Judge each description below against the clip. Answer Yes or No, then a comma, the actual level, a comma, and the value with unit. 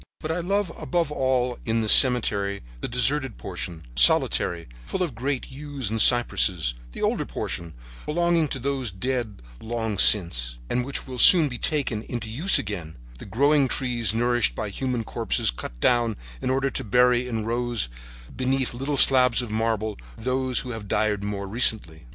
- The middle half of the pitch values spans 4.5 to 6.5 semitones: No, average, 3.8 semitones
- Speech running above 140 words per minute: Yes, average, 170 wpm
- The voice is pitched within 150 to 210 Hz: No, low, 120 Hz